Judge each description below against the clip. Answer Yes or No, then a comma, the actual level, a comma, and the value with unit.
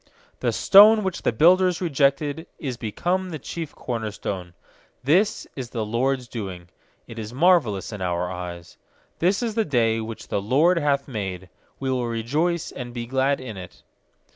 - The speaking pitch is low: Yes, low, 130 Hz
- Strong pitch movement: Yes, wide, 7.1 semitones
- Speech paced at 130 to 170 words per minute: Yes, average, 165 wpm